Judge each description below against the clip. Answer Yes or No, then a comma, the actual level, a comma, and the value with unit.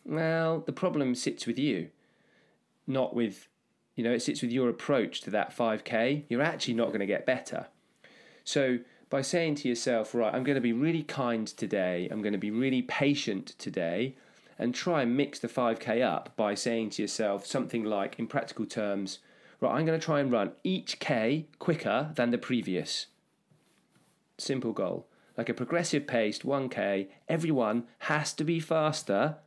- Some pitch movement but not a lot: Yes, average, 4.9 semitones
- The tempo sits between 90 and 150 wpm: No, average, 175 wpm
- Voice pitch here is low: Yes, low, 125 Hz